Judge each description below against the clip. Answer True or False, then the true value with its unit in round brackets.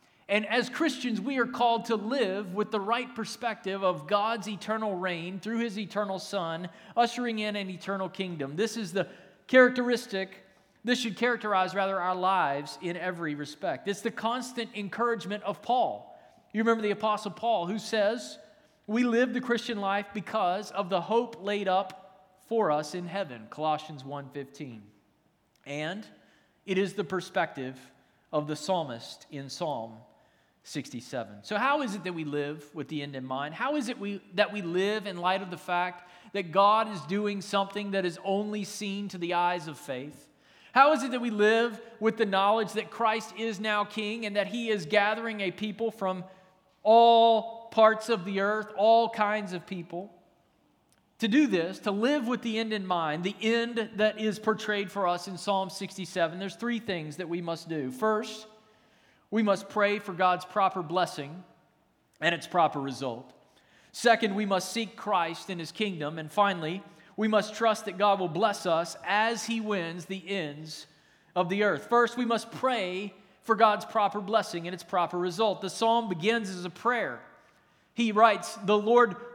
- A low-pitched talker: False (200 Hz)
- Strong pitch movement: False (3.7 semitones)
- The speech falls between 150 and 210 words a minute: True (180 wpm)